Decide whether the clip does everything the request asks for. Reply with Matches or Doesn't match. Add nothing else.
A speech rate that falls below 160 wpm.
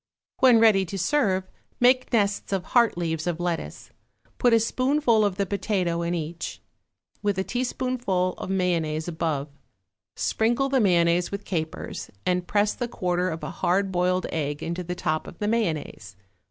Doesn't match